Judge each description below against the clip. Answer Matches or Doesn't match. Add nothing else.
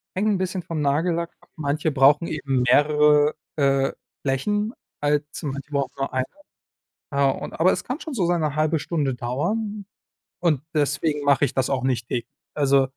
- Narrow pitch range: Doesn't match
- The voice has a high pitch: Doesn't match